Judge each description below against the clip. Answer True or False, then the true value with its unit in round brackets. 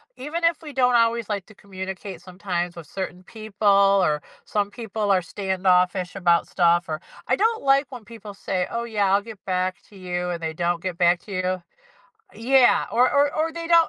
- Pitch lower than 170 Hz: False (195 Hz)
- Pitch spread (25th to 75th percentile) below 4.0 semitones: False (4.4 semitones)